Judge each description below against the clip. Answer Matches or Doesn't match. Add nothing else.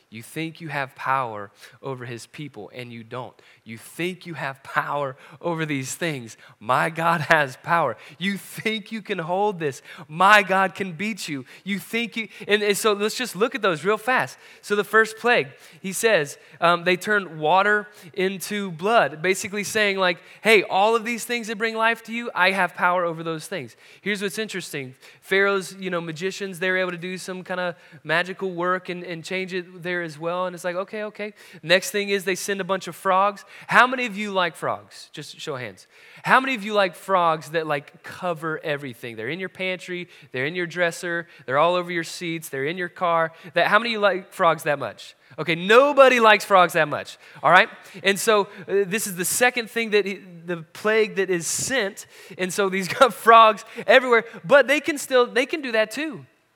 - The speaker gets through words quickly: Matches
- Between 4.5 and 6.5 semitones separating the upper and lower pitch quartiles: Doesn't match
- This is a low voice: Doesn't match